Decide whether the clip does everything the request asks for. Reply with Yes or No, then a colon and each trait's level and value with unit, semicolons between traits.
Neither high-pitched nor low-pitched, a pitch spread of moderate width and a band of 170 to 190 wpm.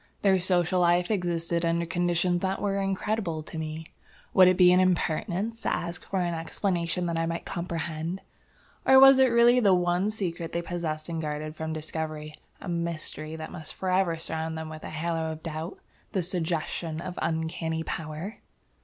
No: medium, 170 Hz; narrow, 2.3 semitones; average, 175 wpm